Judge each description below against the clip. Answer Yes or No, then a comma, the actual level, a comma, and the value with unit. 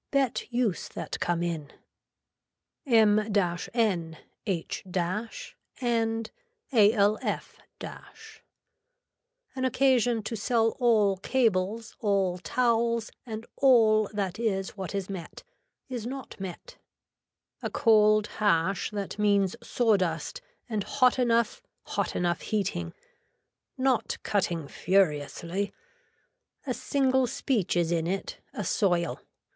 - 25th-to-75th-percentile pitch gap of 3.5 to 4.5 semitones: Yes, average, 4.1 semitones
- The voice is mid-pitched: No, high, 210 Hz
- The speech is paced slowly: Yes, slow, 105 wpm